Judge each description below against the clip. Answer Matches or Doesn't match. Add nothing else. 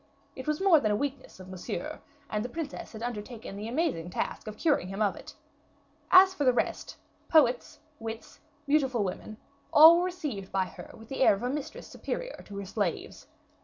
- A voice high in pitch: Matches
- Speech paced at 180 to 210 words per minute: Matches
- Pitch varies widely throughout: Matches